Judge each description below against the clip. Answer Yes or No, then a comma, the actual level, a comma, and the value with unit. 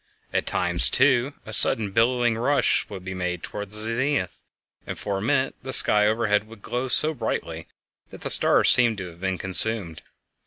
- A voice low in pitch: Yes, low, 110 Hz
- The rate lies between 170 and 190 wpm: Yes, average, 185 wpm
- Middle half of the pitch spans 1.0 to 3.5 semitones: No, average, 4.3 semitones